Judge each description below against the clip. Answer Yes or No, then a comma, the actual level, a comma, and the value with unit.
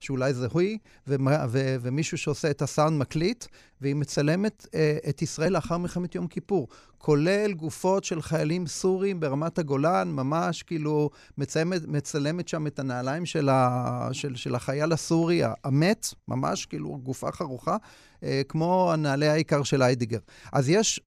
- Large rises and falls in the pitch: No, average, 4.0 semitones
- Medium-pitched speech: Yes, medium, 155 Hz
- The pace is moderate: Yes, average, 140 wpm